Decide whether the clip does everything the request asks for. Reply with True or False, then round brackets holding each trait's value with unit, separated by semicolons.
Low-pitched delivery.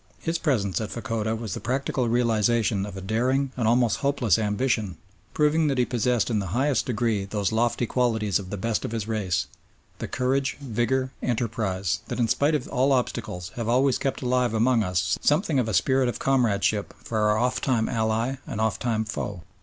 True (115 Hz)